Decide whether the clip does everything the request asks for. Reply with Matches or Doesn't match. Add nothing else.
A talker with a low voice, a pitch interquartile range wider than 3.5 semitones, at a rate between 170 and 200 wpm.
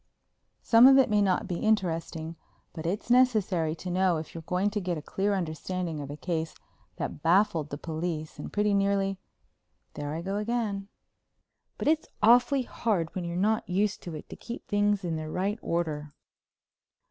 Doesn't match